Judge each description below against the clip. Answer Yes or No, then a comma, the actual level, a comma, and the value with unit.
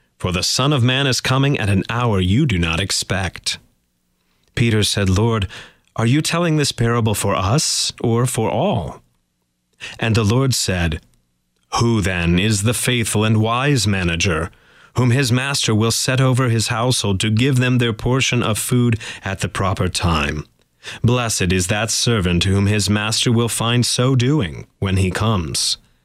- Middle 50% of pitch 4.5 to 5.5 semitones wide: Yes, average, 4.8 semitones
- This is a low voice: Yes, low, 110 Hz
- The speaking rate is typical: Yes, average, 165 wpm